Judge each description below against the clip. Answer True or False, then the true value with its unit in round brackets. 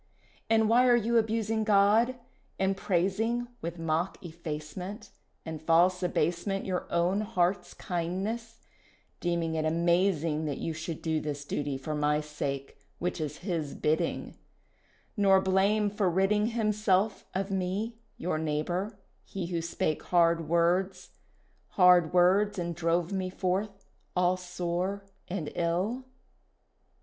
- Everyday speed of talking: False (130 wpm)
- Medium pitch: True (180 Hz)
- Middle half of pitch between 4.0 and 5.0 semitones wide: False (3.3 semitones)